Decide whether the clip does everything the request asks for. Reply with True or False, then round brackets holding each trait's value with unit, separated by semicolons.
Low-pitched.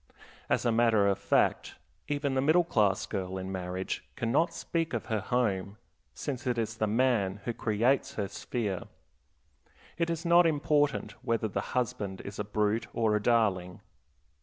True (115 Hz)